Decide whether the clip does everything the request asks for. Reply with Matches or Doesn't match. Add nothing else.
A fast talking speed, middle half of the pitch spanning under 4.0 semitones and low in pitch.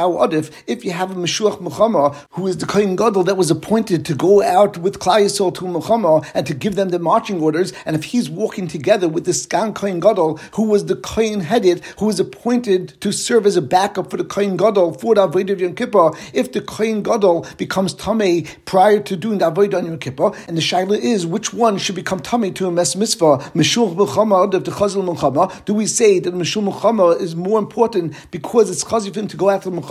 Doesn't match